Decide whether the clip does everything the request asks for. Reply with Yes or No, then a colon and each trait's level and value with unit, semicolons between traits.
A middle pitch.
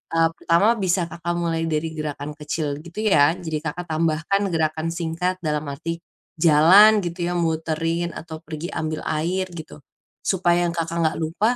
Yes: medium, 165 Hz